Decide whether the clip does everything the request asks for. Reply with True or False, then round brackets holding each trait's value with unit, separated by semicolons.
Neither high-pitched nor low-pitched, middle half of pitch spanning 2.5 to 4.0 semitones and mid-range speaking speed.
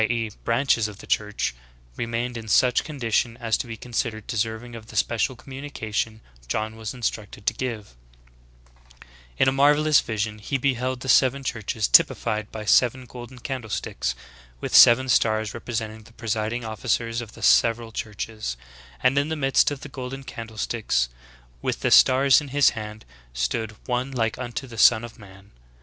False (115 Hz; 2.9 semitones; 170 wpm)